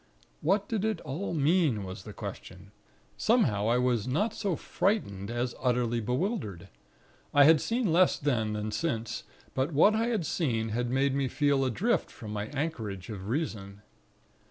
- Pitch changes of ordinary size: No, wide, 7.6 semitones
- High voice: No, low, 130 Hz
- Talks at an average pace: Yes, average, 160 wpm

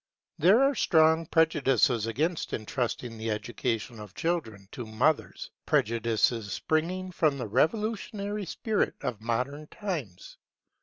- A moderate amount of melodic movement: No, wide, 7.1 semitones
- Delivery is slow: Yes, slow, 115 wpm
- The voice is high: No, medium, 140 Hz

